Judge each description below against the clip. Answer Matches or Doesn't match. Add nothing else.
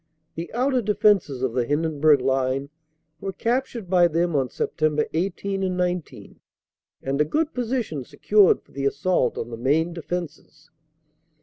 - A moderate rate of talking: Matches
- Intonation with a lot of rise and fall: Matches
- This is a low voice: Doesn't match